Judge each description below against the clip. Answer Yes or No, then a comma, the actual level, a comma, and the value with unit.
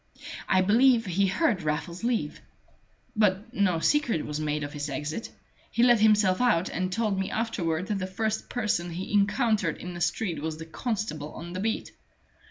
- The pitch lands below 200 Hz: Yes, high, 190 Hz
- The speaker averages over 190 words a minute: No, average, 180 wpm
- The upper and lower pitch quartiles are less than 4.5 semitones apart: No, average, 5.0 semitones